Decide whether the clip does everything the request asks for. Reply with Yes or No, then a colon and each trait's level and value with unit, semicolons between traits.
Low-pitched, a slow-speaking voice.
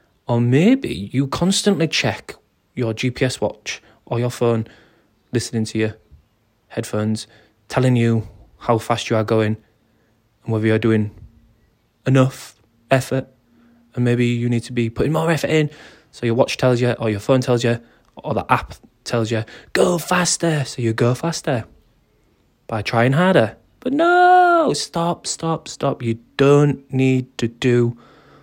No: low, 120 Hz; average, 150 wpm